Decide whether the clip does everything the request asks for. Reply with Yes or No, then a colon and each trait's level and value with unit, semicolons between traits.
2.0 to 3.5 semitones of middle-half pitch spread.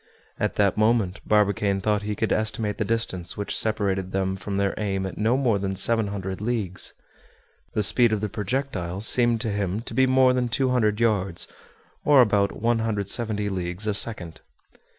Yes: average, 2.8 semitones